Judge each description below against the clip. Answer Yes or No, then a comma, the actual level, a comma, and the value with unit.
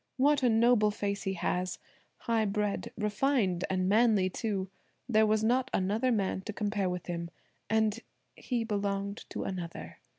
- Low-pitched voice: No, high, 210 Hz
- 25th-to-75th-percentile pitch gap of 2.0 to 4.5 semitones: Yes, average, 2.9 semitones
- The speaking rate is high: No, average, 145 wpm